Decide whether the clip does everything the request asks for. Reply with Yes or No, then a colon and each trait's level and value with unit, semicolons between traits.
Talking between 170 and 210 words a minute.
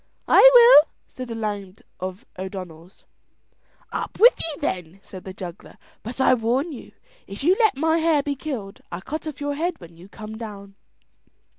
Yes: average, 175 wpm